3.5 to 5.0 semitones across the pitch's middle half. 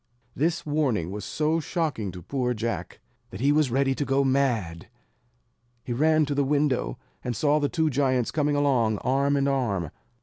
Yes: average, 3.9 semitones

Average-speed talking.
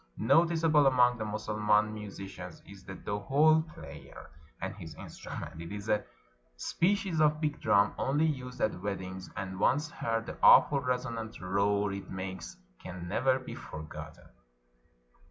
Yes: average, 145 wpm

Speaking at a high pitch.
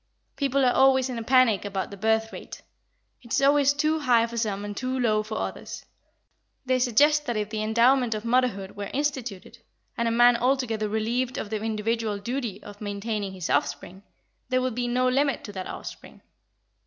Yes: high, 235 Hz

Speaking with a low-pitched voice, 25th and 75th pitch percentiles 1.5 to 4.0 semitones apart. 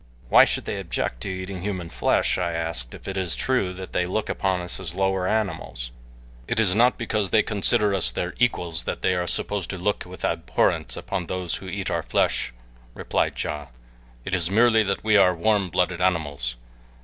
Yes: very low, 95 Hz; average, 2.9 semitones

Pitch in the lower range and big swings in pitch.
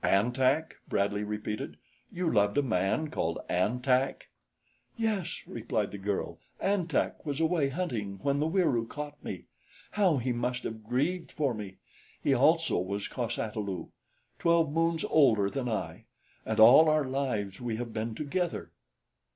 Yes: low, 125 Hz; wide, 6.4 semitones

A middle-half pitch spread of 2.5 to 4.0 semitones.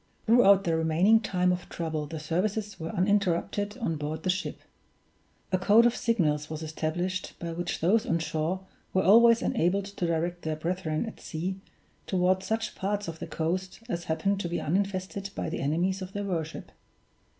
Yes: average, 3.6 semitones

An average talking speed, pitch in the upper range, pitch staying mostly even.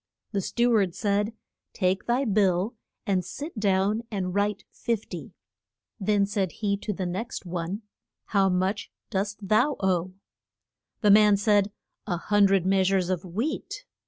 Yes: average, 155 wpm; high, 200 Hz; narrow, 2.1 semitones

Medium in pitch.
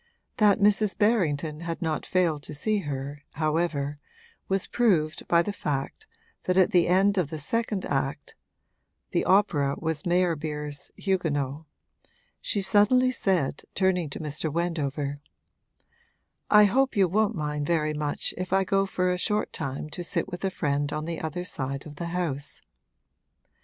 Yes: medium, 170 Hz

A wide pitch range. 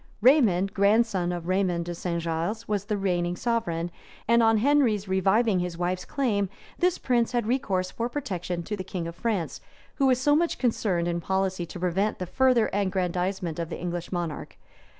No: average, 4.7 semitones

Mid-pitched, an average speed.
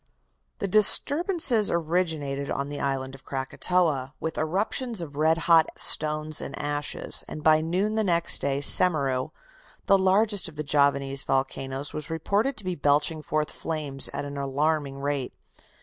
Yes: medium, 155 Hz; average, 150 wpm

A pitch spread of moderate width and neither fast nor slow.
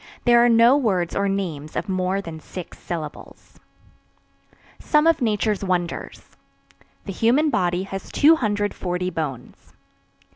No: average, 4.7 semitones; slow, 120 wpm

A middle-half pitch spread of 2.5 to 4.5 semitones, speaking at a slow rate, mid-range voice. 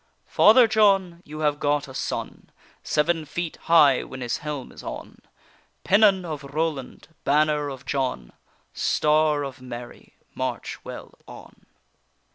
Yes: average, 3.2 semitones; slow, 130 wpm; medium, 150 Hz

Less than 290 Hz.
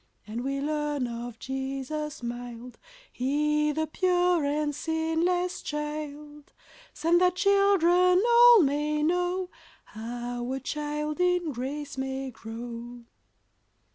No: very high, 295 Hz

